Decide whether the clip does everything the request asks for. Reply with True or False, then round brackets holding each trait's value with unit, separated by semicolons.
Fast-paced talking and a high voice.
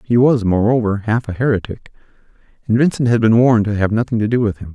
False (230 wpm; 115 Hz)